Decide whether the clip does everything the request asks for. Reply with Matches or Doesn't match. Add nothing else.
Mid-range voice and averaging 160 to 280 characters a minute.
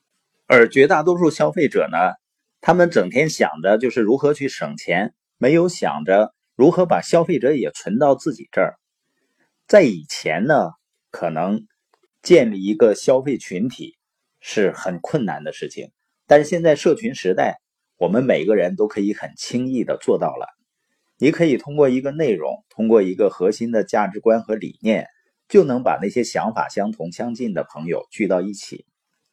Matches